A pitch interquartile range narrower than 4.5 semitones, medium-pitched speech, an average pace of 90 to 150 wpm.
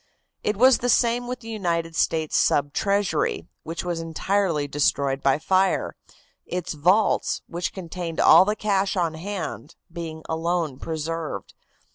Yes: average, 3.8 semitones; medium, 170 Hz; average, 140 wpm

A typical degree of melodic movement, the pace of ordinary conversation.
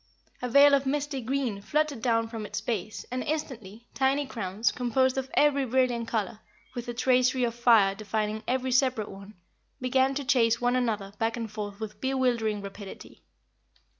Yes: average, 3.4 semitones; average, 165 wpm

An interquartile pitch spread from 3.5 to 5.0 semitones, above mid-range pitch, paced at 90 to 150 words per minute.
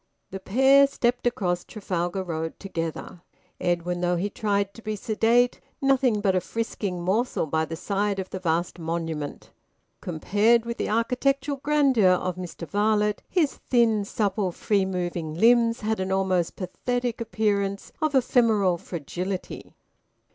Yes: average, 4.7 semitones; high, 200 Hz; average, 140 wpm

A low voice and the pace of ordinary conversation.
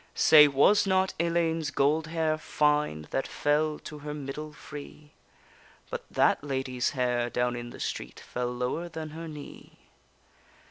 No: medium, 150 Hz; average, 145 wpm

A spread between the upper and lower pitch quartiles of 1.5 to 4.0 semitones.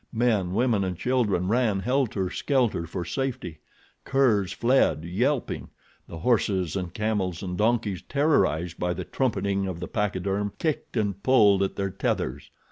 No: average, 4.9 semitones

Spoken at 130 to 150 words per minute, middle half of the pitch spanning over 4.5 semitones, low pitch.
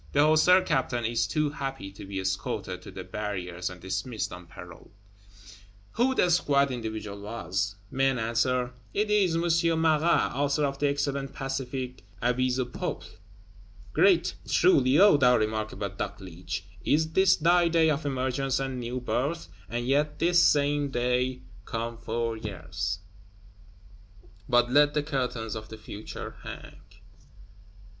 Yes: average, 140 wpm; average, 5.0 semitones; low, 130 Hz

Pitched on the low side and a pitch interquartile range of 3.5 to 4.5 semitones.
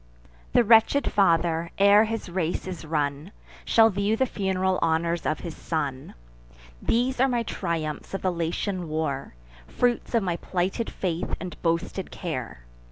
No: medium, 180 Hz; average, 4.2 semitones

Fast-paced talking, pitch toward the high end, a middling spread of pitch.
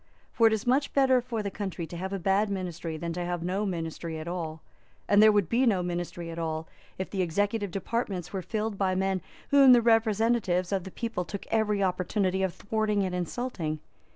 Yes: fast, 210 wpm; high, 195 Hz; average, 3.7 semitones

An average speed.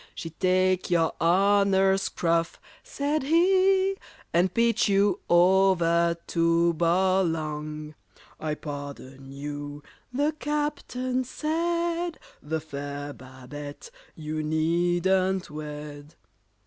No: slow, 90 wpm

